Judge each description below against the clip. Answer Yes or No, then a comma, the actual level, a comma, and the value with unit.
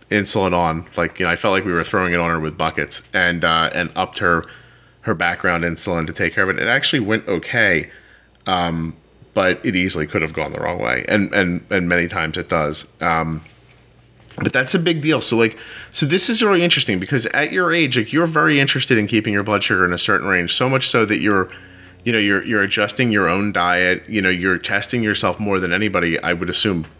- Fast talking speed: Yes, fast, 230 wpm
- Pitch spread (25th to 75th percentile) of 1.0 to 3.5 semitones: No, average, 4.7 semitones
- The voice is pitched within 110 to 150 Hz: No, very low, 95 Hz